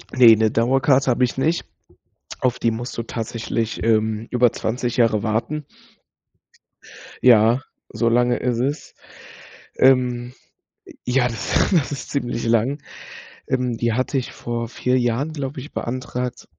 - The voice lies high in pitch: No, low, 120 Hz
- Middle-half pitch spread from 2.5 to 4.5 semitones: No, narrow, 2.0 semitones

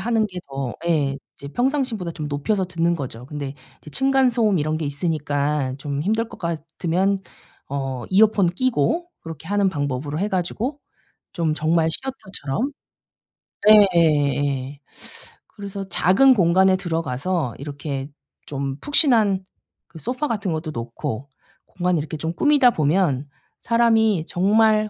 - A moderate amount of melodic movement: No, wide, 6.7 semitones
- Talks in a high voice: No, medium, 170 Hz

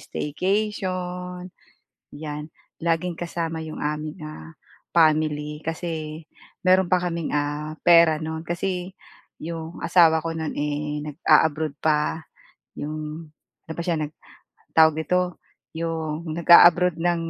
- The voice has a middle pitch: Yes, medium, 160 Hz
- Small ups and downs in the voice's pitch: Yes, narrow, 2.2 semitones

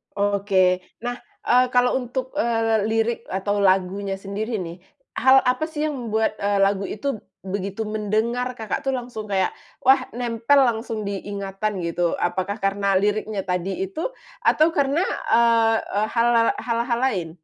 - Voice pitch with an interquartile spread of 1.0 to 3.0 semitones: No, average, 3.7 semitones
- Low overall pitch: No, high, 220 Hz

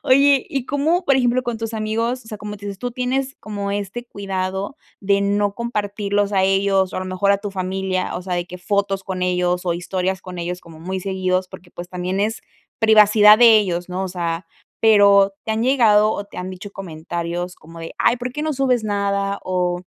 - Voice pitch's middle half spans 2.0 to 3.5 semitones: Yes, average, 3.1 semitones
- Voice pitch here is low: No, high, 200 Hz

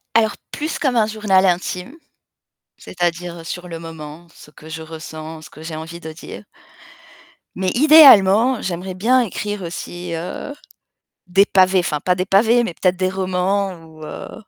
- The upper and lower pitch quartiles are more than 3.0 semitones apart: Yes, average, 3.5 semitones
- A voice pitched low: No, medium, 180 Hz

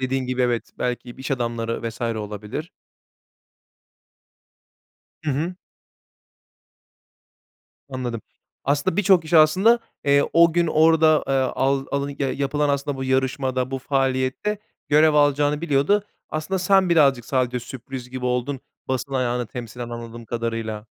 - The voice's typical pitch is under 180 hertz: Yes, low, 135 Hz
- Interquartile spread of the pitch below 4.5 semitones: Yes, average, 3.6 semitones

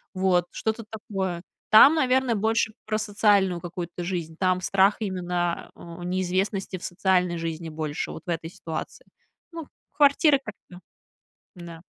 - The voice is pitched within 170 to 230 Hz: Yes, medium, 185 Hz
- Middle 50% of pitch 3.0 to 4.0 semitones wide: Yes, average, 3.6 semitones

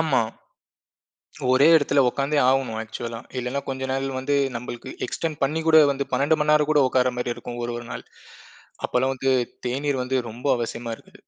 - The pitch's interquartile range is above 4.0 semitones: No, average, 2.8 semitones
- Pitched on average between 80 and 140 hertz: Yes, low, 135 Hz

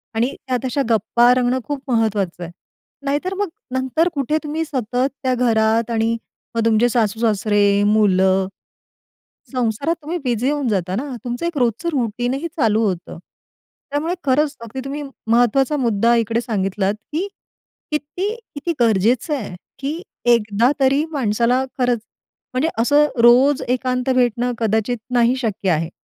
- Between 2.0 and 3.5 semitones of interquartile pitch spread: No, average, 4.0 semitones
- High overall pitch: Yes, high, 245 Hz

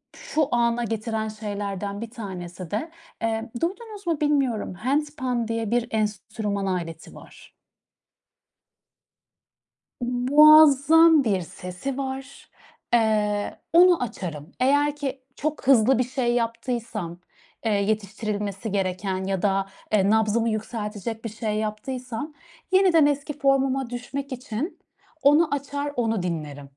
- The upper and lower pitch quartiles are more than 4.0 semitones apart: Yes, average, 5.0 semitones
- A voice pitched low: No, high, 230 Hz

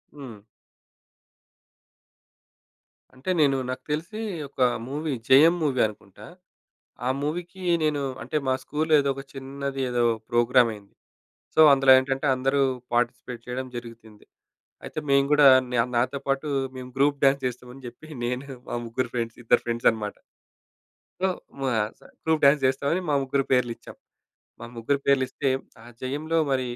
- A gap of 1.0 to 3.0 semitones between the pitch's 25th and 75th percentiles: Yes, average, 2.7 semitones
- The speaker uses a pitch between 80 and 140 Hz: Yes, low, 135 Hz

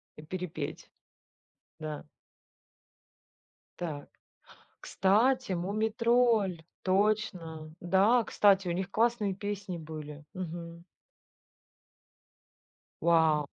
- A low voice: No, medium, 185 Hz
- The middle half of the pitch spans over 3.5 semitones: Yes, average, 4.5 semitones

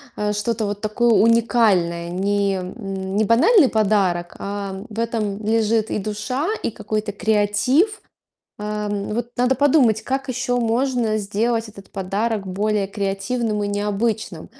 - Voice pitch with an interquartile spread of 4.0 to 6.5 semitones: No, narrow, 2.6 semitones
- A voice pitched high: Yes, high, 215 Hz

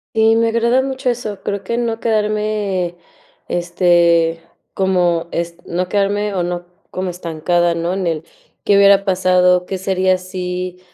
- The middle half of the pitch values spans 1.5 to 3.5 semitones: Yes, average, 2.9 semitones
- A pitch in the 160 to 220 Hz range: Yes, medium, 185 Hz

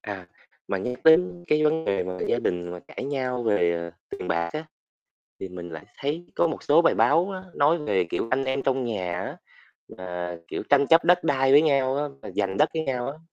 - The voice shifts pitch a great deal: Yes, wide, 8.7 semitones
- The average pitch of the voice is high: No, low, 130 Hz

